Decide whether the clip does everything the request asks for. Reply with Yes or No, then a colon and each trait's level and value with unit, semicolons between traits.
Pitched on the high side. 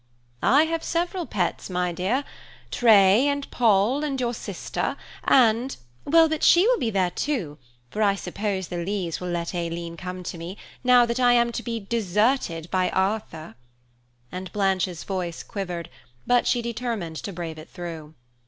Yes: high, 200 Hz